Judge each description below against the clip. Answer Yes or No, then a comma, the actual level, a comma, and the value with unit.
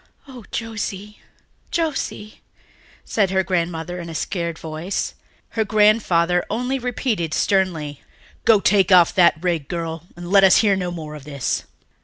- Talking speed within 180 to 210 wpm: No, average, 145 wpm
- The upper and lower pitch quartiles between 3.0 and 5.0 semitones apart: Yes, average, 3.9 semitones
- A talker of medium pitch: Yes, medium, 180 Hz